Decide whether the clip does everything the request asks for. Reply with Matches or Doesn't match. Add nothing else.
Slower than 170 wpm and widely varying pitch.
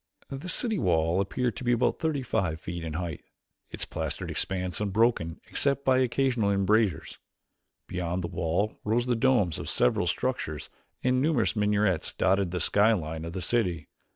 Matches